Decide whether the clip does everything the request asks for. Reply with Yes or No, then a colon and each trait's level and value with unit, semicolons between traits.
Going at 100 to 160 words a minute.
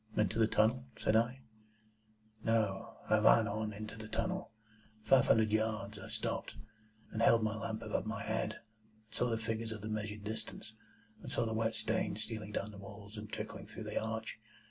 No: average, 190 wpm